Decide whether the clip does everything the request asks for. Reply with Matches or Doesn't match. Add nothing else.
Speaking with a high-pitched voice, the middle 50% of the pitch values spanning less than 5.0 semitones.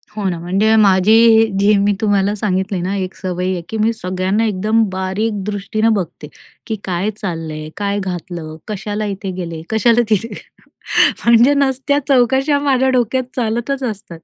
Matches